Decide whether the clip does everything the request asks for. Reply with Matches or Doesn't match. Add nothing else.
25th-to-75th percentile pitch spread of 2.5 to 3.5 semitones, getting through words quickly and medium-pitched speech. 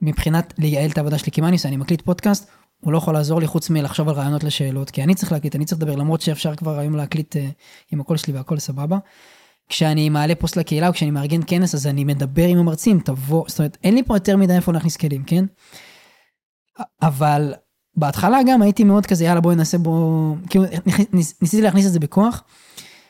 Matches